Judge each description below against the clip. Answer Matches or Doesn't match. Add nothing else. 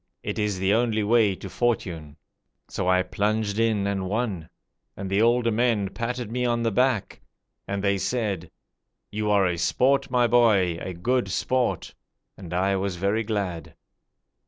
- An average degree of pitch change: Matches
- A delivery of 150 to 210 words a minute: Matches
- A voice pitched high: Doesn't match